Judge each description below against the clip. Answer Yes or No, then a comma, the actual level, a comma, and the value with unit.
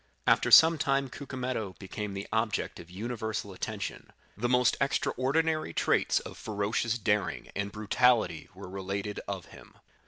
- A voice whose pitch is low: Yes, low, 110 Hz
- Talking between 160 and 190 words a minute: No, slow, 135 wpm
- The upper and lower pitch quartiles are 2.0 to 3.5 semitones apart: No, average, 4.2 semitones